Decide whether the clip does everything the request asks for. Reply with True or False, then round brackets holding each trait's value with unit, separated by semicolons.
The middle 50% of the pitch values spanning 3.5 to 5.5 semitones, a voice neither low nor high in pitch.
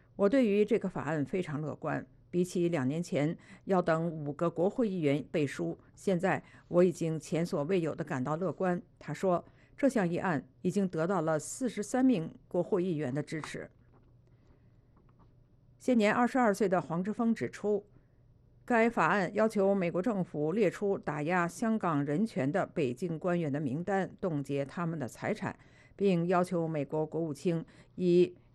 True (5.0 semitones; 170 Hz)